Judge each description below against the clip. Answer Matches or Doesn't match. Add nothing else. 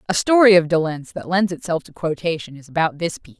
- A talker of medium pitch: Matches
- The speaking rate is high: Matches